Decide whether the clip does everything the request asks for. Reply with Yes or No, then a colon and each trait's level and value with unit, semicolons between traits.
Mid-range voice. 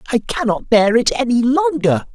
No: high, 225 Hz